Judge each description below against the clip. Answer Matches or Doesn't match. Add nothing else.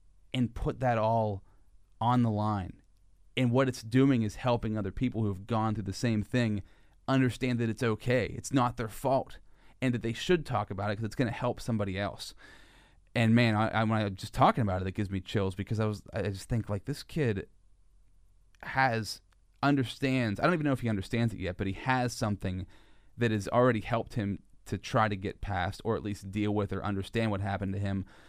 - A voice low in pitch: Matches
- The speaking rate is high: Matches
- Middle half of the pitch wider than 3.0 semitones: Matches